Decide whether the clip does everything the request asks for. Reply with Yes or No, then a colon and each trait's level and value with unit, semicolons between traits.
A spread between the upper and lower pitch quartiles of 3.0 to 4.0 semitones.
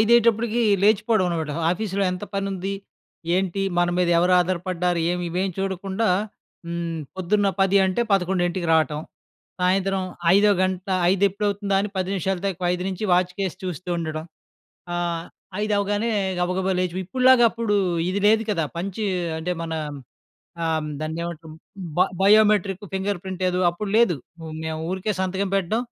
No: narrow, 2.5 semitones